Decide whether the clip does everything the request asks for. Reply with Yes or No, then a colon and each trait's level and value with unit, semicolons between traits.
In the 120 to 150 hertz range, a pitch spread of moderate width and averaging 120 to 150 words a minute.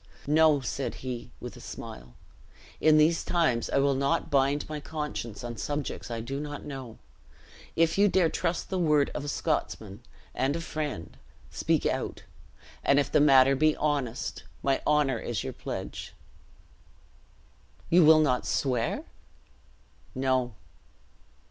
Yes: medium, 140 Hz; average, 3.1 semitones; average, 140 wpm